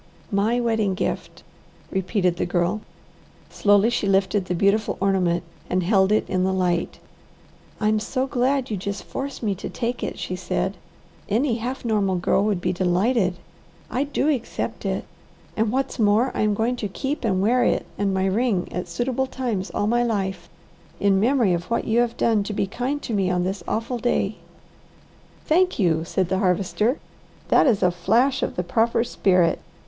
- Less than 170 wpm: No, average, 180 wpm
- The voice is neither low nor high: No, high, 205 Hz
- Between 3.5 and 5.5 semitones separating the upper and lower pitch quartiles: Yes, average, 4.2 semitones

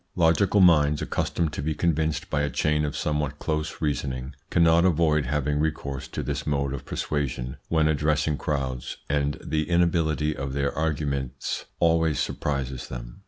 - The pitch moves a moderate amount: No, narrow, 2.1 semitones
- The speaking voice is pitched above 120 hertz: No, very low, 75 Hz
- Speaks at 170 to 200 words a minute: No, average, 155 wpm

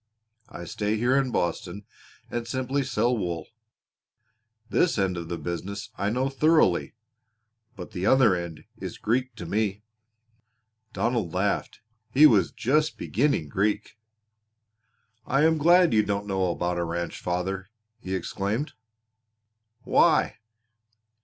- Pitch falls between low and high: No, low, 105 Hz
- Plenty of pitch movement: Yes, wide, 6.2 semitones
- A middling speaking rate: No, slow, 125 wpm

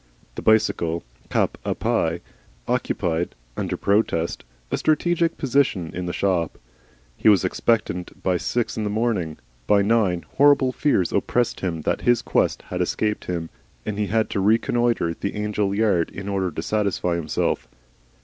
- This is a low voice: Yes, low, 100 Hz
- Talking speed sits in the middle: Yes, average, 155 wpm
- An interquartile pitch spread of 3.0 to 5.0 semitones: Yes, average, 4.5 semitones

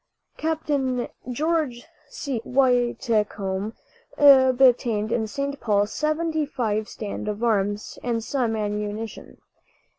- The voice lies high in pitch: Yes, high, 235 Hz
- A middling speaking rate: No, slow, 95 wpm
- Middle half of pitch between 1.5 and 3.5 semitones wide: No, average, 4.6 semitones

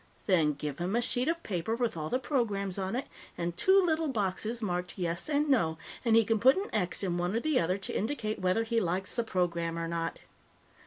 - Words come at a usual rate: No, fast, 225 wpm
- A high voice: Yes, high, 200 Hz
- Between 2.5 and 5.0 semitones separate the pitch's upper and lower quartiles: No, wide, 5.5 semitones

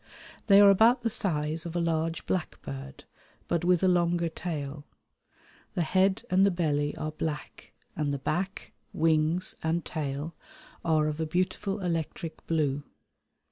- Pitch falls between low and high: Yes, medium, 165 Hz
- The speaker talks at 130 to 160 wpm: Yes, average, 145 wpm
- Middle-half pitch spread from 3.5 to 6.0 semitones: No, average, 3.0 semitones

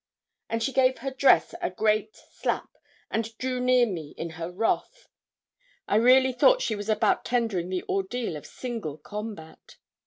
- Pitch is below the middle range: No, high, 220 Hz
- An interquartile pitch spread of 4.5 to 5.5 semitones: Yes, average, 5.0 semitones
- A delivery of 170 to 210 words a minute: No, average, 160 wpm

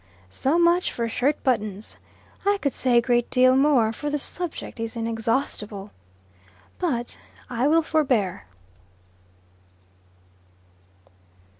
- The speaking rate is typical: No, slow, 110 wpm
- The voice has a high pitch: Yes, very high, 250 Hz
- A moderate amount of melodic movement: Yes, average, 4.6 semitones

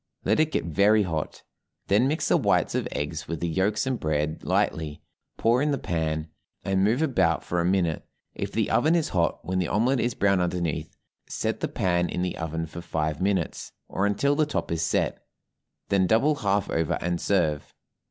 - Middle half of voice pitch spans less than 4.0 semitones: No, average, 4.8 semitones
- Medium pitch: No, very low, 90 Hz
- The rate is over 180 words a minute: Yes, average, 195 wpm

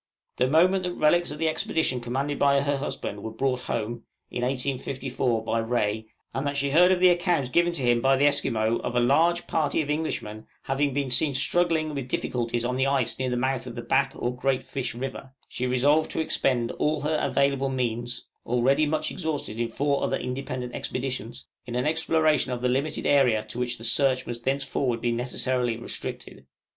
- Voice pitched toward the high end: No, low, 130 Hz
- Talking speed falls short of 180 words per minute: No, average, 195 wpm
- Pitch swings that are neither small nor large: Yes, average, 3.2 semitones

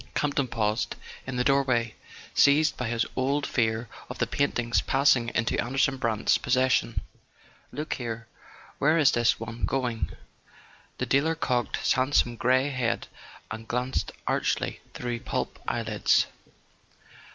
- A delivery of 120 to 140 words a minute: Yes, slow, 135 wpm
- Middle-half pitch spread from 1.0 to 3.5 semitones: Yes, average, 2.8 semitones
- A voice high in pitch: No, low, 125 Hz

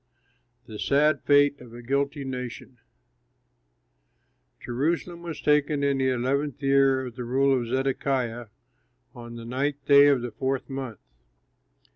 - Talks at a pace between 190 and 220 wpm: No, slow, 135 wpm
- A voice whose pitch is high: No, low, 135 Hz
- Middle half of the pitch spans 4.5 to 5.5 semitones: No, narrow, 2.4 semitones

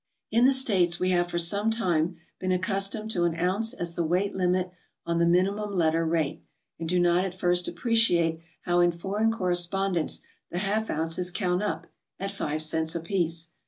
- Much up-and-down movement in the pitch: No, average, 2.7 semitones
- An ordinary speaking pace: Yes, average, 180 wpm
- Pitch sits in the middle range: Yes, medium, 180 Hz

